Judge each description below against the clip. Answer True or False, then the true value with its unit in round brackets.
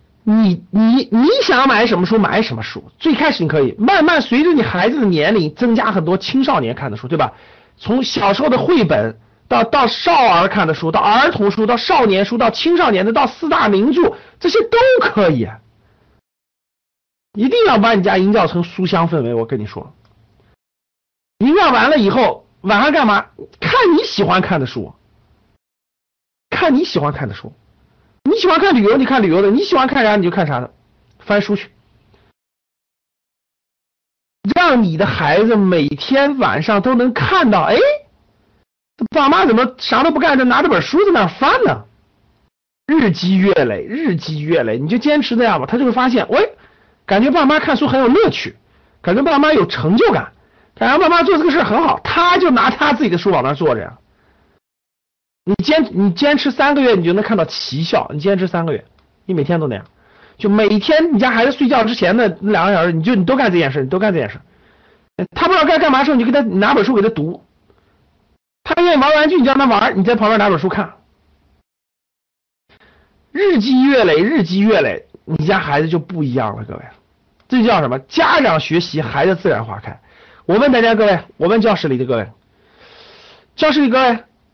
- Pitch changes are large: True (7.6 semitones)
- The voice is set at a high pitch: True (220 Hz)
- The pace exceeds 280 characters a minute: False (275 characters per minute)